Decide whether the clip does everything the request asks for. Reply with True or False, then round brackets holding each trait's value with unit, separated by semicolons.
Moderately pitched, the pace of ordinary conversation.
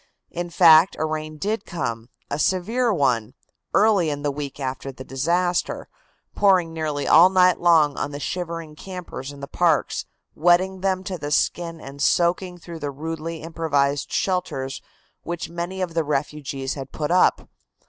True (165 Hz; 160 wpm)